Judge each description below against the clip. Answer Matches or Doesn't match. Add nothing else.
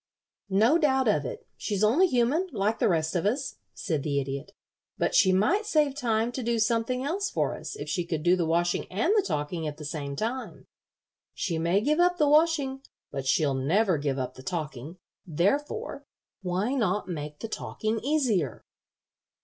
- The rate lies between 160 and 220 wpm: Matches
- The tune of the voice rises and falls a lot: Matches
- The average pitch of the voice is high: Matches